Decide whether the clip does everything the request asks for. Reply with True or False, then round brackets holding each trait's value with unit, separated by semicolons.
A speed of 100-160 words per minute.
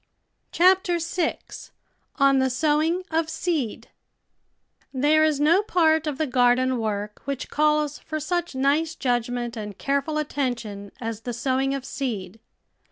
True (140 wpm)